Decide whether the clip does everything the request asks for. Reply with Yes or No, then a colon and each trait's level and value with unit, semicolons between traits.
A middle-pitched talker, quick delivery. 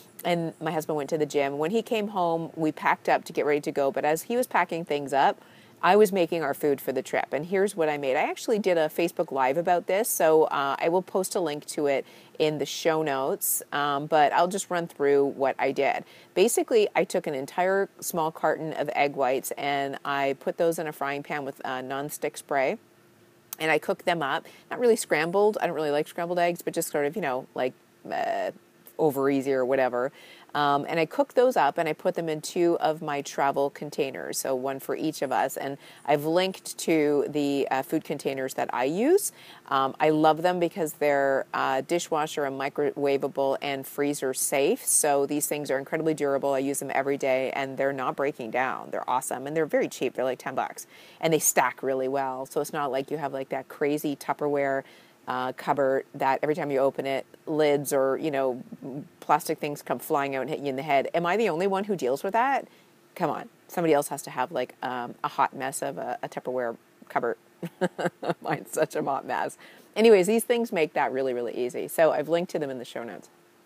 Yes: medium, 150 Hz; fast, 225 wpm